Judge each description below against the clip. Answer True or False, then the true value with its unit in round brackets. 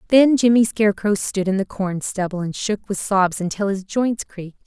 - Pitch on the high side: True (200 Hz)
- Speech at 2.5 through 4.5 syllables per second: False (5.0 syllables/s)